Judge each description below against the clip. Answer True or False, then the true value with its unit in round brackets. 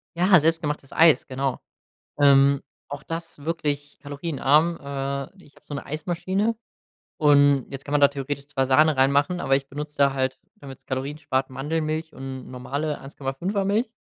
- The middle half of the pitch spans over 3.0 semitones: False (2.6 semitones)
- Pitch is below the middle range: False (145 Hz)